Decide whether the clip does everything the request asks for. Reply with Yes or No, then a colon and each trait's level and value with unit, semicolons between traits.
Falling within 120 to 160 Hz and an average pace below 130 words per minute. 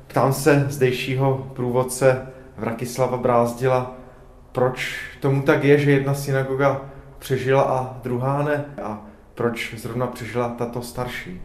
Yes: low, 130 Hz; average, 120 wpm